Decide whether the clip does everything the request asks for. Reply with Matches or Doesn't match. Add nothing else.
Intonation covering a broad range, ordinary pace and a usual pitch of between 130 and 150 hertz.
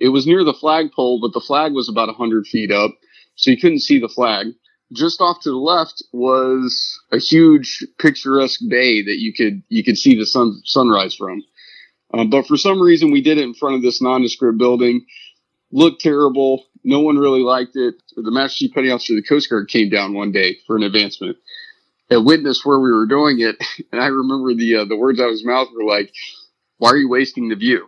Doesn't match